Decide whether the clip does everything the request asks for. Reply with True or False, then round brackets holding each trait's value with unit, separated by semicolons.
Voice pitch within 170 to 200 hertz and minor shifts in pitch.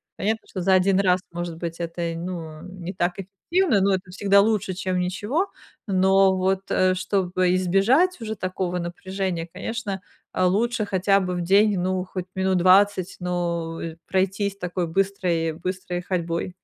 True (185 Hz; 1.8 semitones)